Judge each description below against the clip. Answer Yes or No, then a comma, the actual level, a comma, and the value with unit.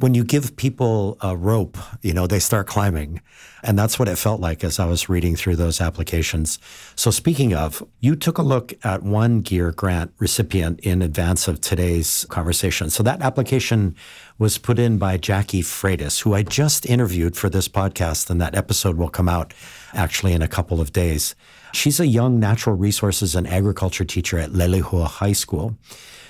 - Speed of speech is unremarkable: Yes, average, 185 wpm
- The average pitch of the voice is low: Yes, very low, 95 Hz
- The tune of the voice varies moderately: Yes, average, 4.2 semitones